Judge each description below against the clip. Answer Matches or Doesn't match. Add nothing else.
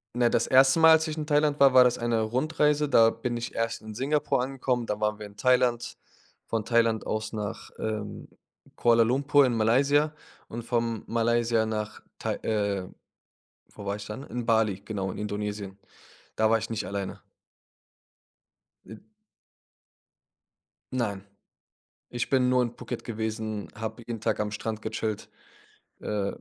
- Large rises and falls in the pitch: Doesn't match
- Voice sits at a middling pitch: Doesn't match